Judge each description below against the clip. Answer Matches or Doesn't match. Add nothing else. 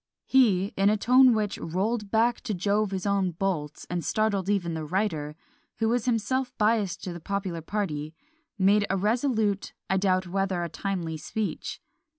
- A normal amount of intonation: Matches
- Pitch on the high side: Matches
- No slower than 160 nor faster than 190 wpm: Matches